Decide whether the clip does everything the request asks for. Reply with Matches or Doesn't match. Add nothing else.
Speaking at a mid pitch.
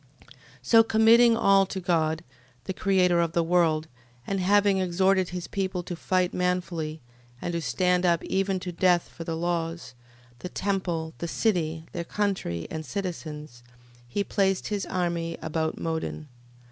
Matches